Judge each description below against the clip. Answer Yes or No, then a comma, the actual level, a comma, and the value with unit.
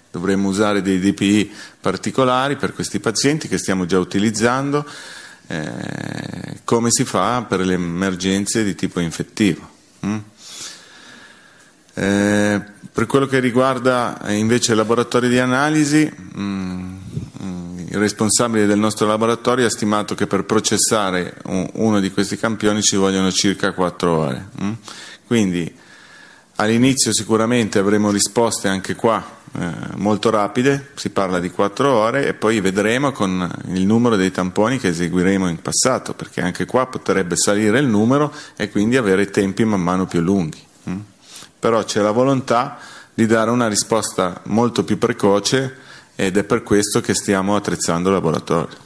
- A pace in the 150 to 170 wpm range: No, average, 140 wpm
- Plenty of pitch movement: No, average, 3.5 semitones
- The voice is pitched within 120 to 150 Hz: No, low, 105 Hz